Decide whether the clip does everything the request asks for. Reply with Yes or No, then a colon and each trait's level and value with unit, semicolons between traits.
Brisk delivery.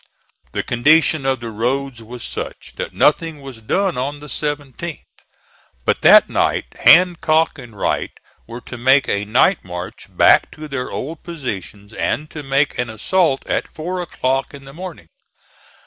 No: average, 160 wpm